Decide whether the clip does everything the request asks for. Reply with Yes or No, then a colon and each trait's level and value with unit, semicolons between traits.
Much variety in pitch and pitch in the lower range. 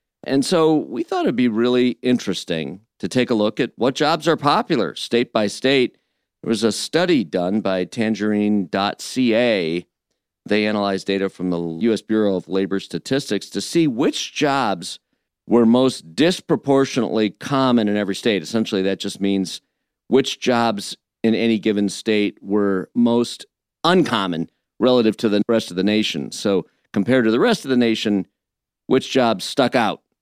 No: average, 3.7 semitones; low, 110 Hz